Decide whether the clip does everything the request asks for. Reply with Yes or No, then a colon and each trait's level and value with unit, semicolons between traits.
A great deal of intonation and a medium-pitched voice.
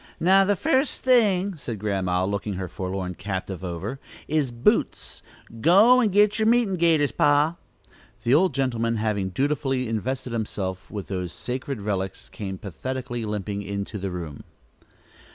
No: wide, 8.5 semitones; low, 115 Hz